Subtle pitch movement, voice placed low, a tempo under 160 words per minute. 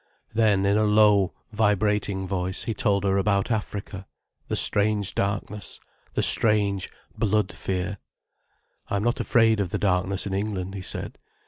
Yes: narrow, 1.7 semitones; low, 100 Hz; average, 150 wpm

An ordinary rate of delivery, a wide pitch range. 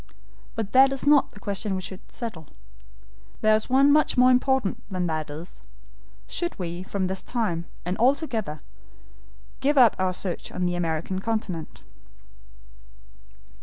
Yes: average, 155 wpm; wide, 6.1 semitones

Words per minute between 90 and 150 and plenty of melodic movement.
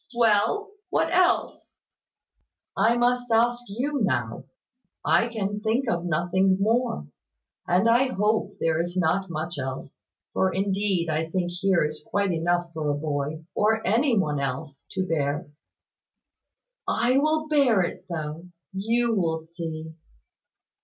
Yes: slow, 135 wpm; wide, 6.1 semitones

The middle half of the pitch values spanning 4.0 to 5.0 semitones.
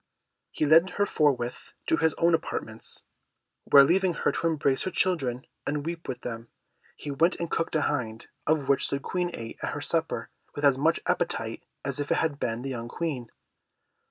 Yes: average, 4.3 semitones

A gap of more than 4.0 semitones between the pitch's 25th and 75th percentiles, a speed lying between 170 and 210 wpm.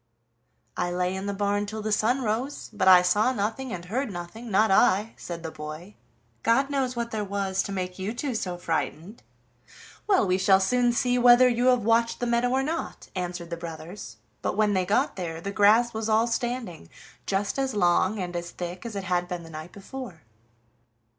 Yes: average, 4.8 semitones; average, 200 wpm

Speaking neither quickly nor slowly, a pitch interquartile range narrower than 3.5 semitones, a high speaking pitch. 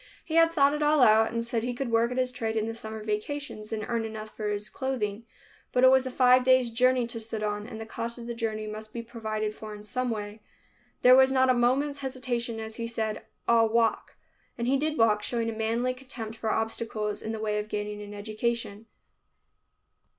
No: fast, 220 wpm; average, 2.7 semitones; high, 230 Hz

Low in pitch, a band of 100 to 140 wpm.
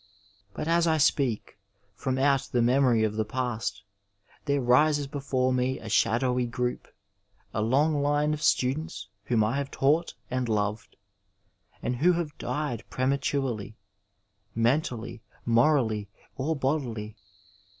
Yes: low, 130 Hz; slow, 135 wpm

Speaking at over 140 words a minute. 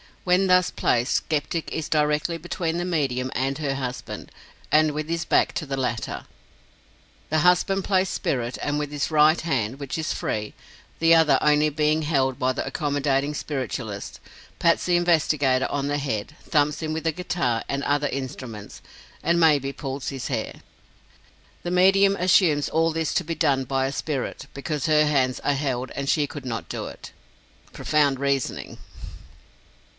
Yes: average, 170 wpm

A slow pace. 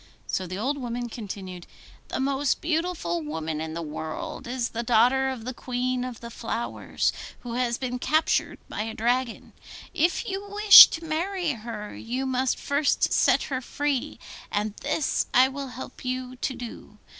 No: average, 170 wpm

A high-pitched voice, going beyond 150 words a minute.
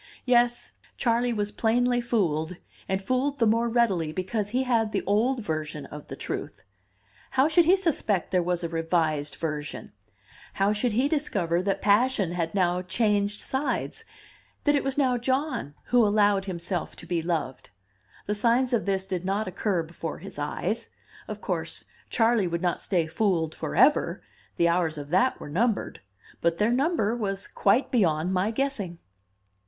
Yes: high, 205 Hz; average, 165 wpm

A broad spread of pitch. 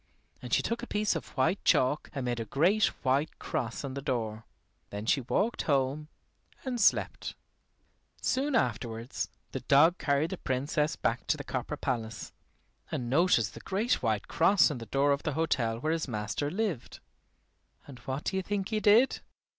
Yes: wide, 6.9 semitones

